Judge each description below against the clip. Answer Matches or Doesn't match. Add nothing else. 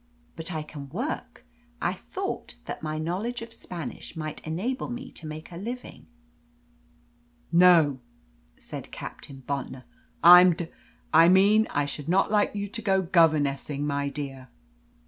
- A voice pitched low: Doesn't match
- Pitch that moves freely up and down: Doesn't match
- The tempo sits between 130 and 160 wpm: Matches